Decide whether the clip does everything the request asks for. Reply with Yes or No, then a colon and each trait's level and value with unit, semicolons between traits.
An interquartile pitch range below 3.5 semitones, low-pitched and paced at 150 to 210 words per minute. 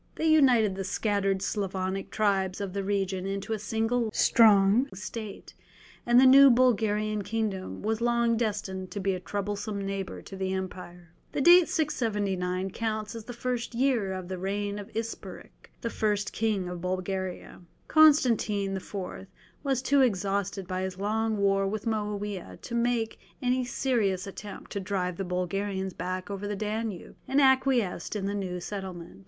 No: average, 3.0 semitones; high, 205 Hz; average, 160 wpm